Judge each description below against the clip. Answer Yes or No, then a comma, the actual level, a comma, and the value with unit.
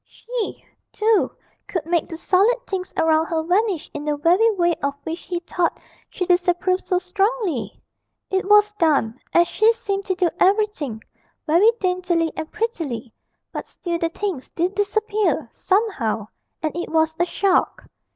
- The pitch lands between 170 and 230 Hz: No, very high, 360 Hz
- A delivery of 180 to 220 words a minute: No, average, 155 wpm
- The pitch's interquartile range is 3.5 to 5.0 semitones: Yes, average, 4.1 semitones